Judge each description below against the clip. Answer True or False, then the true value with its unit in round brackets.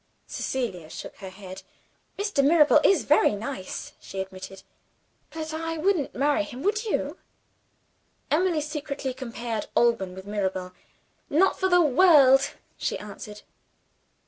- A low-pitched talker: False (270 Hz)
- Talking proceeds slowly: True (125 wpm)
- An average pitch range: False (7.7 semitones)